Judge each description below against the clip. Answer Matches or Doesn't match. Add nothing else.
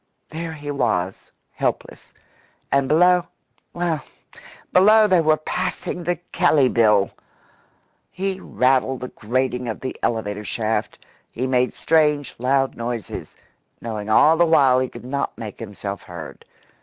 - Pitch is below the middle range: Matches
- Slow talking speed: Matches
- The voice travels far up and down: Matches